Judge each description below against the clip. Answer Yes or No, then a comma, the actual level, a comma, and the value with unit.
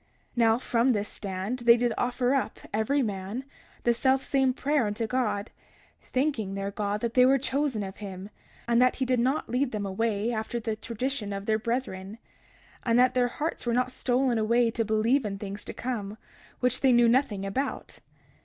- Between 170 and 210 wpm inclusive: Yes, average, 190 wpm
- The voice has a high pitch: Yes, high, 235 Hz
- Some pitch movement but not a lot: Yes, average, 3.4 semitones